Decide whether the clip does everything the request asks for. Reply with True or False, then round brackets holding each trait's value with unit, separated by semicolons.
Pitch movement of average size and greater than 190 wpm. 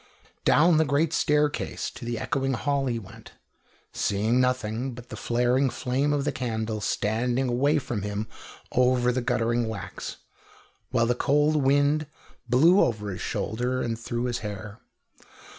False (3.4 semitones; 150 wpm)